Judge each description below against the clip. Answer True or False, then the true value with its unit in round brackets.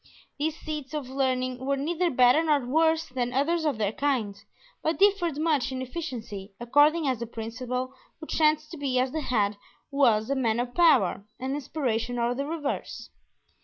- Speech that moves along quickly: False (175 wpm)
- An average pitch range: True (4.0 semitones)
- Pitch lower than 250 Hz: False (265 Hz)